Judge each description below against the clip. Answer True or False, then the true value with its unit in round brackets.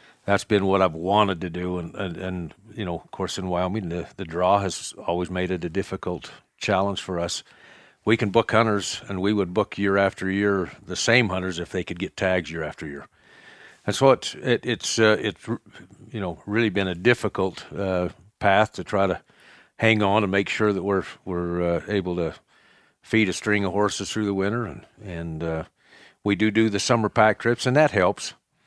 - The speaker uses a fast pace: True (215 wpm)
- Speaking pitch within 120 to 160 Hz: False (100 Hz)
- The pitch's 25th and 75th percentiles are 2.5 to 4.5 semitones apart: True (2.9 semitones)